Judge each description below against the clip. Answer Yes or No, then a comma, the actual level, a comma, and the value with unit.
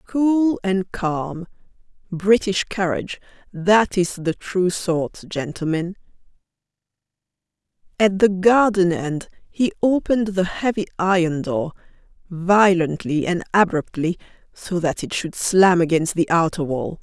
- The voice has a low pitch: No, medium, 185 Hz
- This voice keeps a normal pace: No, slow, 115 wpm